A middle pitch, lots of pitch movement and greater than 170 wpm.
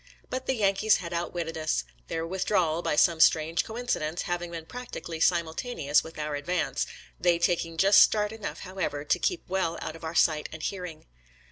No: medium, 170 Hz; average, 3.2 semitones; average, 190 wpm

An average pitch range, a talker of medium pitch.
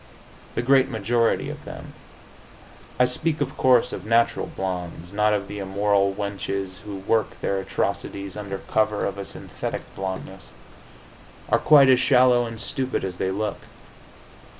No: average, 3.9 semitones; low, 105 Hz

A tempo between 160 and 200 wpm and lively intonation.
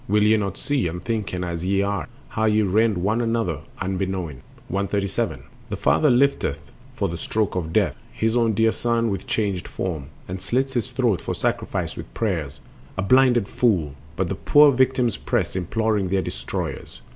No: average, 175 wpm; average, 4.2 semitones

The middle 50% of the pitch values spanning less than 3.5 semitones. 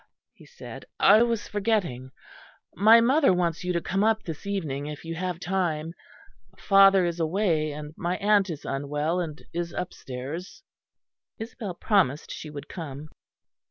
No: average, 4.6 semitones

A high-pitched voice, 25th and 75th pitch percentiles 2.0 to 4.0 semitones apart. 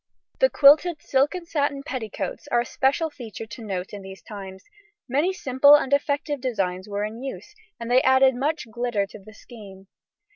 No: very high, 250 Hz; wide, 5.4 semitones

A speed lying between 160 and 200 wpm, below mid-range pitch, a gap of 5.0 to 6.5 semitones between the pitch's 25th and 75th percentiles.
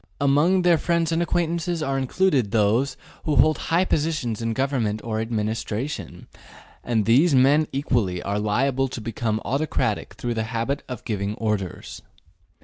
No: average, 145 wpm; low, 130 Hz; wide, 5.6 semitones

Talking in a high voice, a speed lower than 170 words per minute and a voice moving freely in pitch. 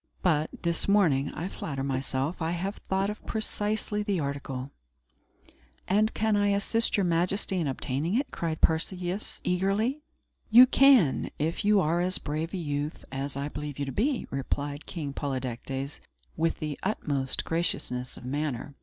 No: medium, 165 Hz; average, 155 wpm; wide, 6.0 semitones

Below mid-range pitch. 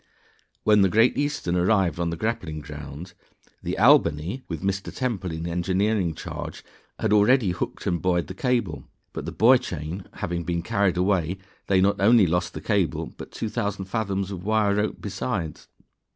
Yes: very low, 95 Hz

